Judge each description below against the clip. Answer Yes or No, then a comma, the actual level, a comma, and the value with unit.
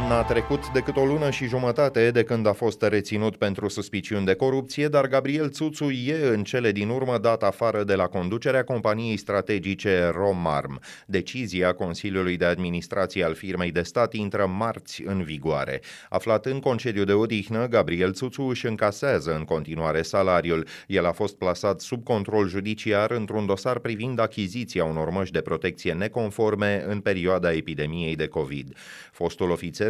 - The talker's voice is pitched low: Yes, low, 105 Hz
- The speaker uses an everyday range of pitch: Yes, average, 4.8 semitones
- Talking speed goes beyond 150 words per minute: Yes, average, 160 wpm